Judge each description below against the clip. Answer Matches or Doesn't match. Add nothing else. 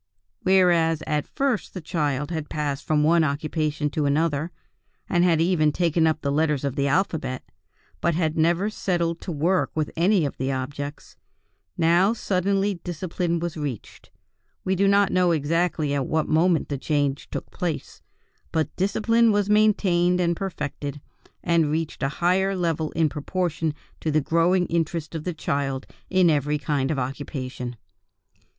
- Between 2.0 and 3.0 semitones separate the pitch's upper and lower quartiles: Doesn't match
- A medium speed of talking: Matches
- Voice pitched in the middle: Matches